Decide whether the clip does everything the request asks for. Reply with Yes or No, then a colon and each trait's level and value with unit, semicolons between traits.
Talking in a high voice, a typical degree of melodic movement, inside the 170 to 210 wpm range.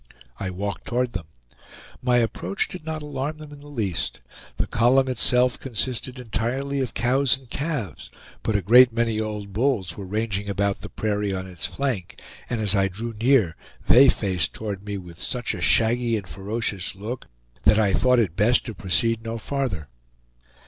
No: low, 115 Hz; average, 4.3 semitones; average, 175 wpm